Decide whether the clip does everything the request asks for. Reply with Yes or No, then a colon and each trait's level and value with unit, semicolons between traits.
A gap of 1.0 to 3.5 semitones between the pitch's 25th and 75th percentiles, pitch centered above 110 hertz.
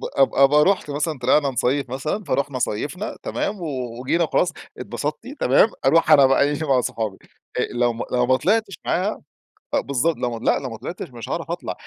No: average, 4.6 semitones; medium, 140 Hz